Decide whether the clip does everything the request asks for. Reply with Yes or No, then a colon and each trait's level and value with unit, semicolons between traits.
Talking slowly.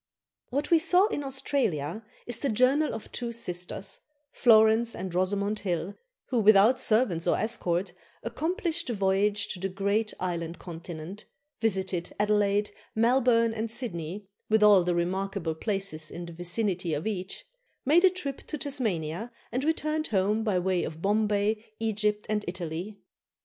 No: average, 150 wpm